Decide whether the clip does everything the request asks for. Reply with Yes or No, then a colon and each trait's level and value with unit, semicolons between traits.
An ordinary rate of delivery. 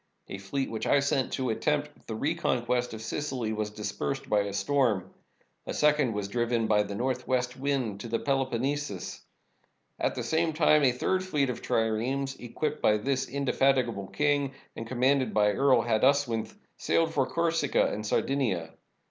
Yes: average, 165 wpm